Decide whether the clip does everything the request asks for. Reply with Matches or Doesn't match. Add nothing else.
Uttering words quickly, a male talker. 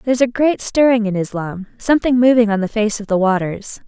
Doesn't match